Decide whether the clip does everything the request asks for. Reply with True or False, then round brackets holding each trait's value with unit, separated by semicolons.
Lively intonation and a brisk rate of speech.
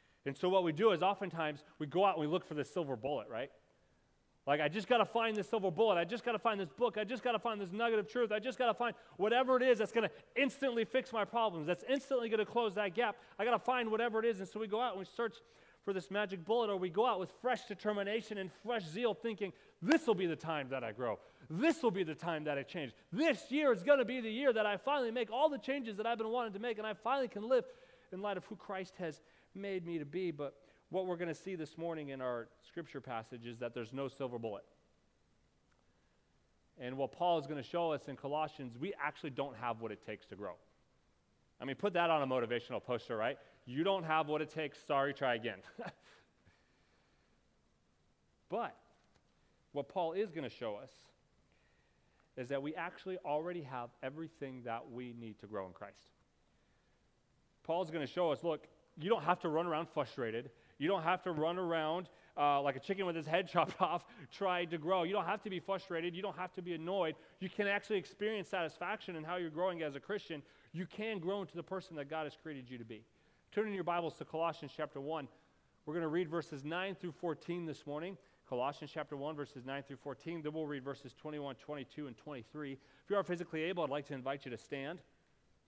True (6.4 semitones; 235 wpm)